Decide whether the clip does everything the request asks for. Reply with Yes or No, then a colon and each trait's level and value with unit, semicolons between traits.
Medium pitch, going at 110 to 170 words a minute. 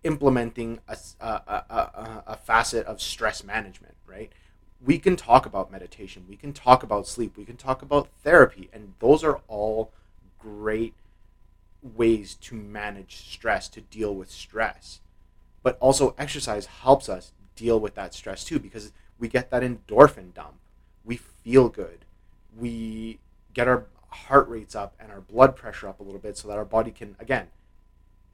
No: low, 110 Hz; average, 165 wpm